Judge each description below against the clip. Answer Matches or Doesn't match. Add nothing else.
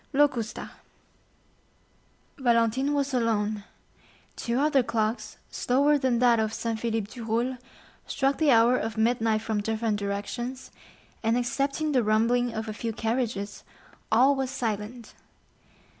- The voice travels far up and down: Doesn't match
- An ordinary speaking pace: Doesn't match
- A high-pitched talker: Matches